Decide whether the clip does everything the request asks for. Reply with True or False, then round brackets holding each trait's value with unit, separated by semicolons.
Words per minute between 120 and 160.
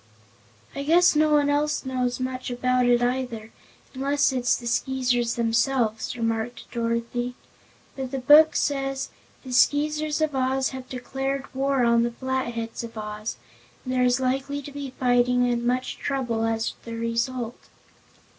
True (150 wpm)